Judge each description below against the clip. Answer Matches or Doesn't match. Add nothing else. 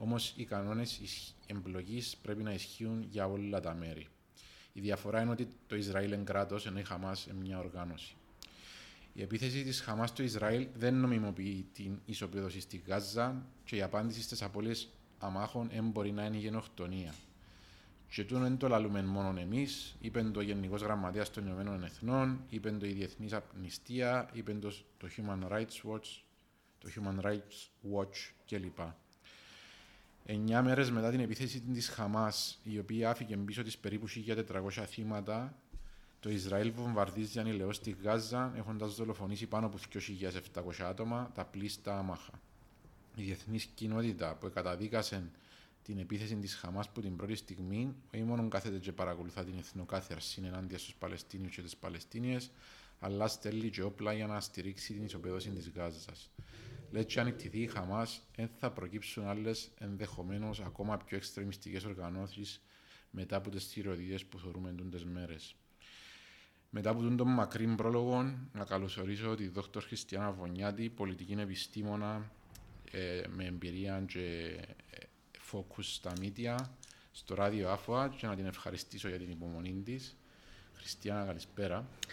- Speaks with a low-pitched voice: Matches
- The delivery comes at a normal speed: Matches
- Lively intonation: Doesn't match